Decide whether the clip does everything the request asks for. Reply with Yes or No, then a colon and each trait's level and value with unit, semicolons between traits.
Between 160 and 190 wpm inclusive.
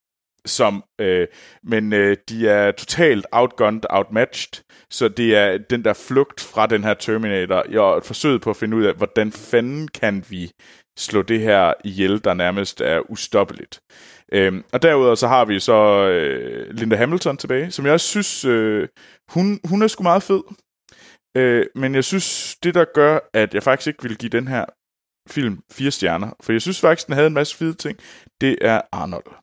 Yes: average, 185 wpm